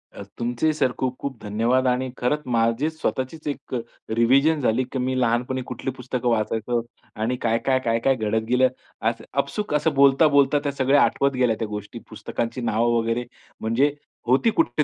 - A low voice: Yes, low, 125 Hz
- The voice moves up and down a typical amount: Yes, average, 3.0 semitones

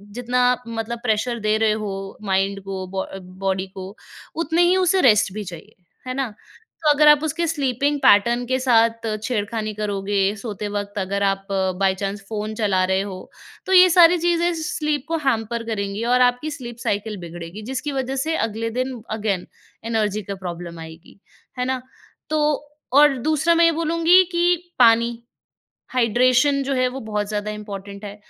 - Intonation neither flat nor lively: No, wide, 5.9 semitones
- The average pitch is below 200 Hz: No, high, 230 Hz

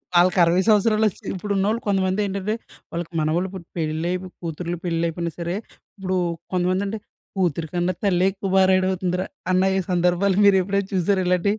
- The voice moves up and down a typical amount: No, narrow, 1.9 semitones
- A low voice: No, medium, 185 Hz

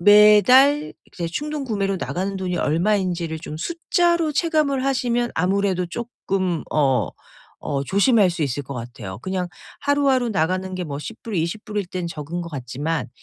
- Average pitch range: No, wide, 6.6 semitones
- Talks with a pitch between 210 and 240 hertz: No, high, 190 Hz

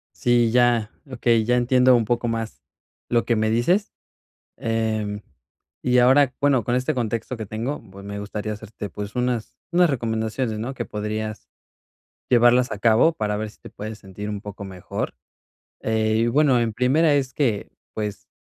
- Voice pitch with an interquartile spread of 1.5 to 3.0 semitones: Yes, average, 2.7 semitones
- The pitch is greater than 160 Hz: No, low, 115 Hz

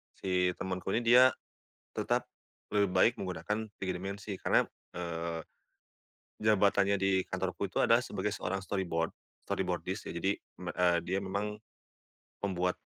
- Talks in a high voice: No, very low, 95 Hz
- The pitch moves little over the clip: Yes, narrow, 2.0 semitones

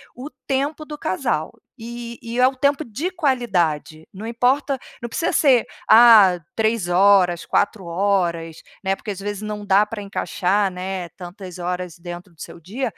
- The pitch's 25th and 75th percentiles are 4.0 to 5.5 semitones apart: Yes, average, 5.1 semitones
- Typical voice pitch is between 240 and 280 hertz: No, high, 205 Hz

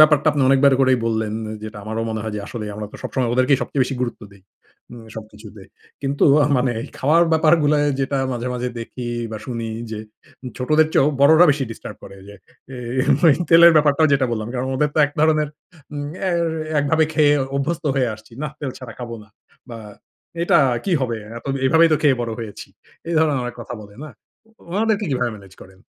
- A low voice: Yes, low, 130 Hz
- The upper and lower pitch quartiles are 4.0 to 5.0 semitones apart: Yes, average, 4.5 semitones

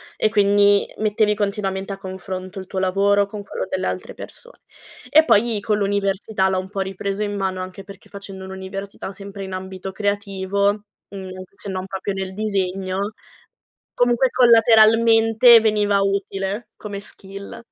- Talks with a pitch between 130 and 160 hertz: No, high, 200 Hz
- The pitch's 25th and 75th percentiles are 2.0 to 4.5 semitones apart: No, narrow, 1.6 semitones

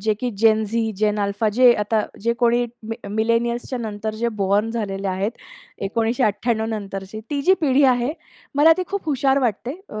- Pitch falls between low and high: No, high, 225 Hz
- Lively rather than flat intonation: No, average, 2.8 semitones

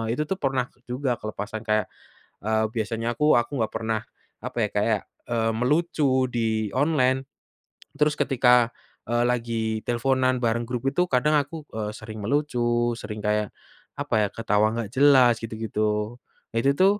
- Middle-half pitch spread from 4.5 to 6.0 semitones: No, average, 3.5 semitones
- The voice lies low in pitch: Yes, low, 120 Hz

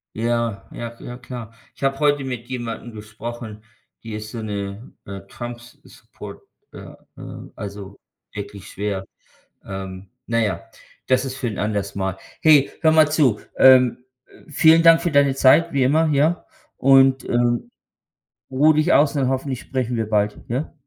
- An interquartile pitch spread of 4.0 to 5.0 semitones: Yes, average, 4.3 semitones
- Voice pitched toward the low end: Yes, low, 120 Hz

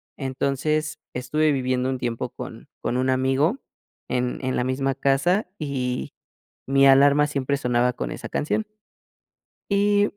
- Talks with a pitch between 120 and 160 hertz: Yes, low, 135 Hz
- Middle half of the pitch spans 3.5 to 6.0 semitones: No, narrow, 2.6 semitones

